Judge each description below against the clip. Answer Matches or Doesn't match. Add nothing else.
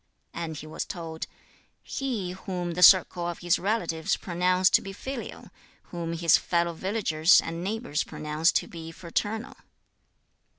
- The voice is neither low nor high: Matches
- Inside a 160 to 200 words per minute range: Doesn't match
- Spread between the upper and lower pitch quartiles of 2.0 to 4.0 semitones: Matches